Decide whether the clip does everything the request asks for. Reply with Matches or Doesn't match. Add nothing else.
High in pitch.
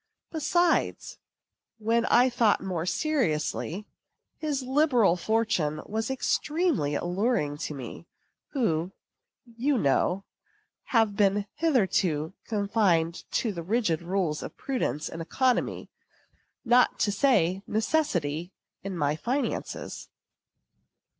Matches